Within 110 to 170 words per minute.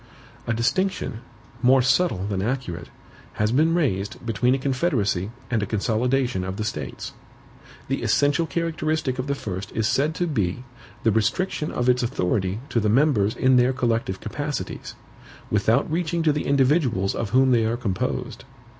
Yes: average, 160 wpm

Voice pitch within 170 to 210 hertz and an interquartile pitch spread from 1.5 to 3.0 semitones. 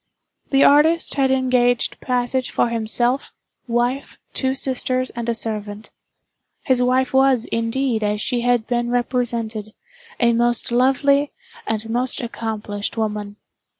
No: high, 240 Hz; narrow, 2.5 semitones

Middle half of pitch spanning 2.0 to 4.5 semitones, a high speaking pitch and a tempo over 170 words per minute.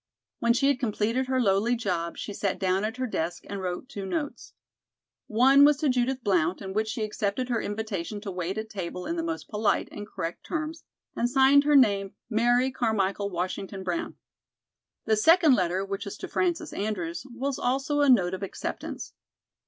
No: average, 5.1 semitones; high, 220 Hz; average, 185 wpm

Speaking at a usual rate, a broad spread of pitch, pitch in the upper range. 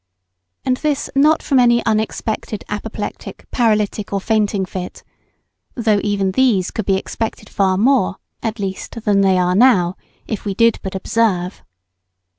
No: average, 145 wpm; average, 3.1 semitones; high, 210 Hz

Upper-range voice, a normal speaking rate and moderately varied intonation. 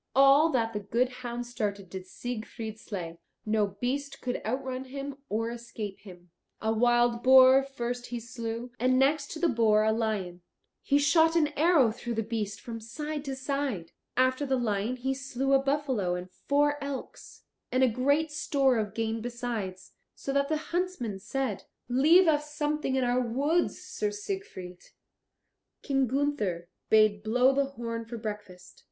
Yes: high, 245 Hz; average, 165 wpm; average, 4.2 semitones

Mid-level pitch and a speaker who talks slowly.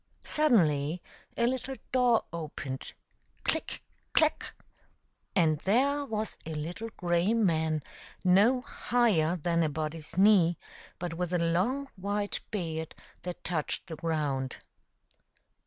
Yes: medium, 175 Hz; slow, 125 wpm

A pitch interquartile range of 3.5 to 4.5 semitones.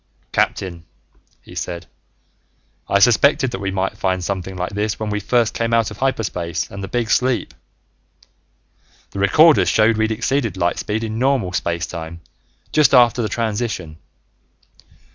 Yes: average, 4.0 semitones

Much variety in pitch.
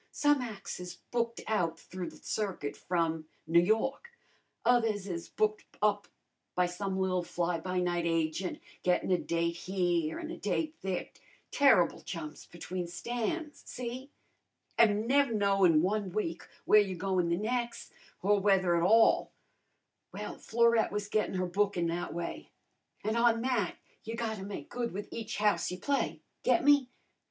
No: average, 4.7 semitones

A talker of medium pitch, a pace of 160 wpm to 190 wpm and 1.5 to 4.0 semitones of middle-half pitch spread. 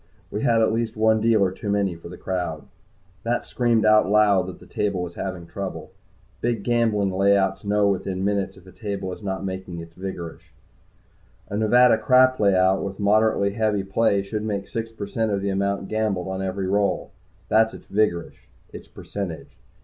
No: low, 100 Hz; average, 180 wpm; narrow, 2.4 semitones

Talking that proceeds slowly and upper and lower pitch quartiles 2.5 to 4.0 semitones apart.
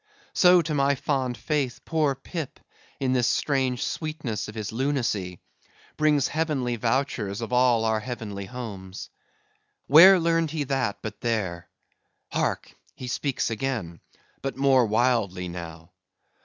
No: slow, 130 wpm; average, 4.7 semitones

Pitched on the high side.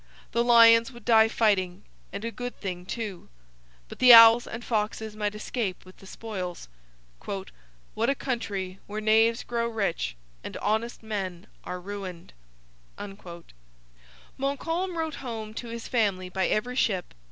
Yes: high, 215 Hz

